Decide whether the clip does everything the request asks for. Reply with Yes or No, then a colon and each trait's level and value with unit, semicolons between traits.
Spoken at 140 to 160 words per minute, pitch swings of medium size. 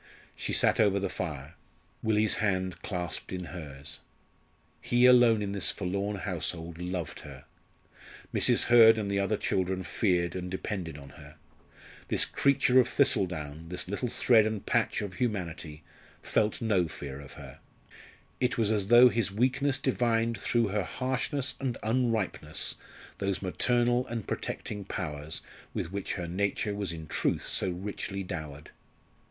Yes: average, 150 wpm; average, 4.5 semitones